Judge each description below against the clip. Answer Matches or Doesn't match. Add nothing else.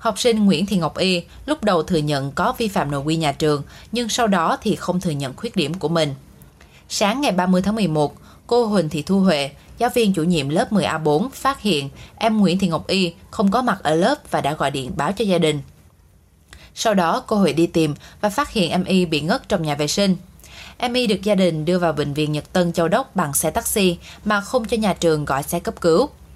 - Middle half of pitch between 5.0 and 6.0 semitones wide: Matches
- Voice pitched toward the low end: Doesn't match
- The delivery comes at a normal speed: Matches